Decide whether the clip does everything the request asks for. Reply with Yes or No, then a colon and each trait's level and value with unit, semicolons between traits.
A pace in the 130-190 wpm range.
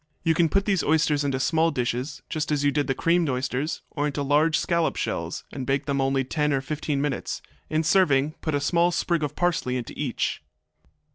No: fast, 205 wpm